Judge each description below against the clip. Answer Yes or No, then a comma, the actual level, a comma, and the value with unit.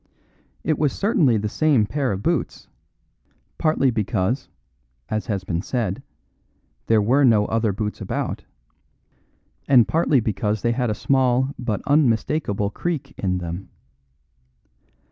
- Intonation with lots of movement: No, average, 4.9 semitones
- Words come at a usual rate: No, slow, 125 wpm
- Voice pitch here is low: Yes, low, 115 Hz